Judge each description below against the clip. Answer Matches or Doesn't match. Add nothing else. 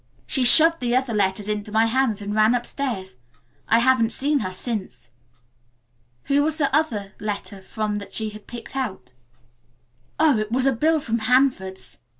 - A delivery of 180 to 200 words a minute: Doesn't match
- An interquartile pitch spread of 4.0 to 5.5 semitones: Matches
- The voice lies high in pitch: Matches